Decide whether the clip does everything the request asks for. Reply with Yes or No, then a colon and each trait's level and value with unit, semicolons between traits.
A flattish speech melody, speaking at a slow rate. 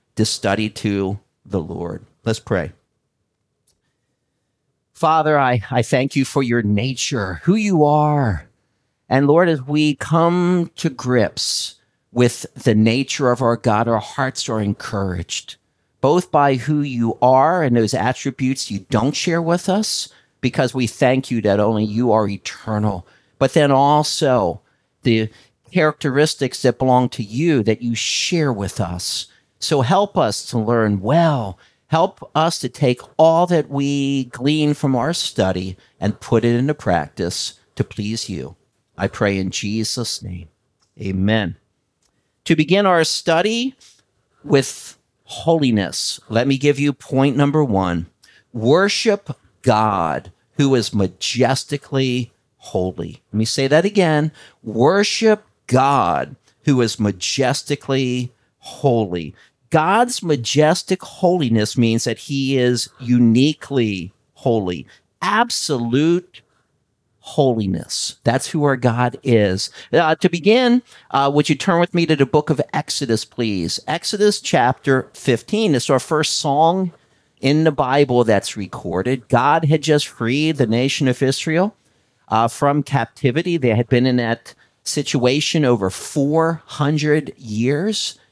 No: average, 5.1 semitones; slow, 130 wpm